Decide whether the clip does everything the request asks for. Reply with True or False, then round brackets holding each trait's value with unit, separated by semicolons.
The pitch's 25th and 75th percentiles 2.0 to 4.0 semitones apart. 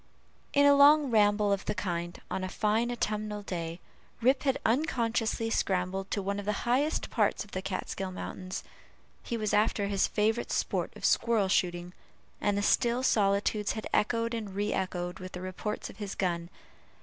True (3.4 semitones)